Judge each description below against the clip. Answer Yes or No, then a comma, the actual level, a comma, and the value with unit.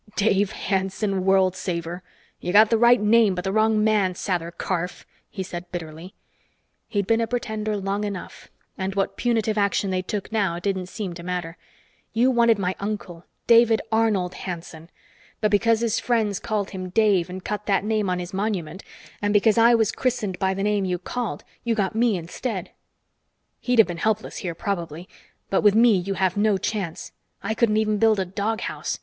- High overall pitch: Yes, high, 200 Hz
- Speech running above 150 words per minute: Yes, average, 185 wpm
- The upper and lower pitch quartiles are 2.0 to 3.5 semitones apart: Yes, average, 3.0 semitones